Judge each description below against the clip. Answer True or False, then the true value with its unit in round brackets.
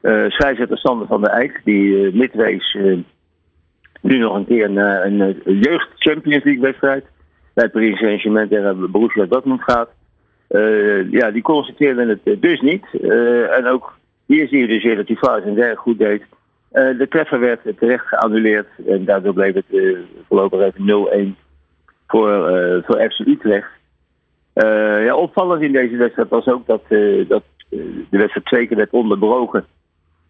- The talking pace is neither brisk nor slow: True (180 wpm)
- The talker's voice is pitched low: True (110 Hz)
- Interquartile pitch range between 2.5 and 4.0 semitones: False (5.1 semitones)